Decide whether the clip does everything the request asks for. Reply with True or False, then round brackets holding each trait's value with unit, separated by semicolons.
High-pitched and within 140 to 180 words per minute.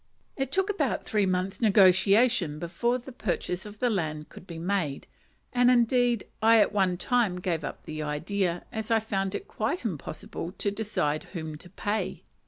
True (200 Hz; 175 wpm)